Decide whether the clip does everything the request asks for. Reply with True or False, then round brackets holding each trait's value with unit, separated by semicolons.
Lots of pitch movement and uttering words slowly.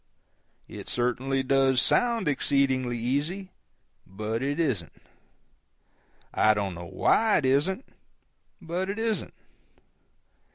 True (6.8 semitones; 100 wpm)